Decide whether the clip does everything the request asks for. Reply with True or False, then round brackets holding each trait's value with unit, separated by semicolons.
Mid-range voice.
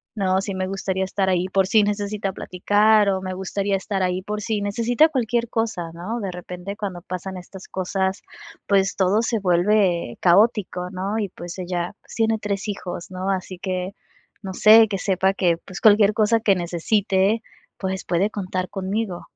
False (195 Hz)